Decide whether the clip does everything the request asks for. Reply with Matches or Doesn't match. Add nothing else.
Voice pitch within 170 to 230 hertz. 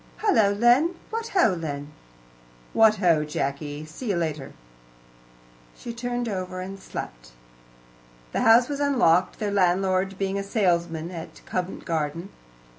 Matches